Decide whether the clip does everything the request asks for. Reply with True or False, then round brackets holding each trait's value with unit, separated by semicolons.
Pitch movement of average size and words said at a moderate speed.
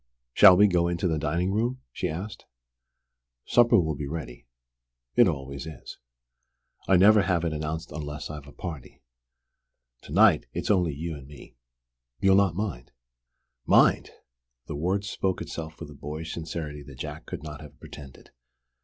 True (3.7 semitones; 160 wpm)